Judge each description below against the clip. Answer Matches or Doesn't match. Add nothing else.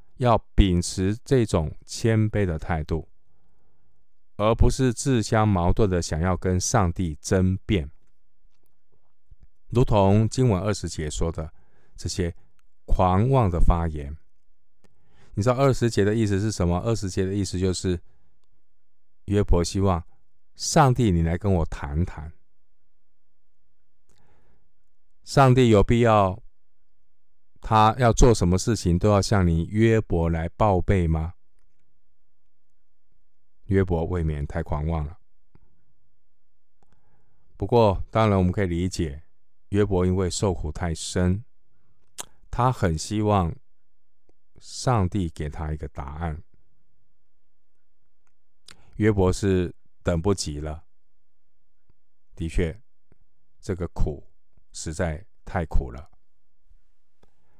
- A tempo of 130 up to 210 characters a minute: Matches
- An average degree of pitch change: Matches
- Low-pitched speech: Matches